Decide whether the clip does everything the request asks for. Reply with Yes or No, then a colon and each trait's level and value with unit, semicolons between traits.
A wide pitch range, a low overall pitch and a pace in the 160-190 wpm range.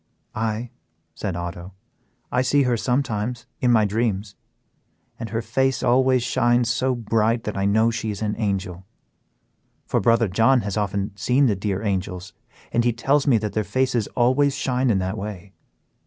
No: average, 3.5 semitones; low, 115 Hz; average, 170 wpm